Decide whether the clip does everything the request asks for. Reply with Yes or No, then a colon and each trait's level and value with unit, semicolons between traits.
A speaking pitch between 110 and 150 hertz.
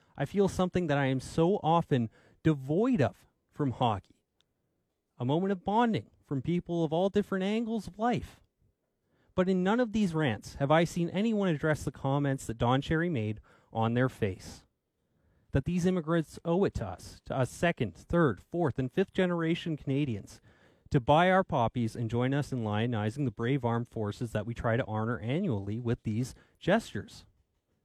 Yes: medium, 140 Hz